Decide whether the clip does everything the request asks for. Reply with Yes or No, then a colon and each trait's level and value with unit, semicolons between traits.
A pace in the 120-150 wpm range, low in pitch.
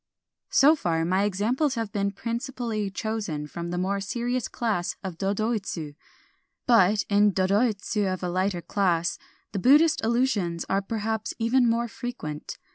No: average, 140 wpm; high, 205 Hz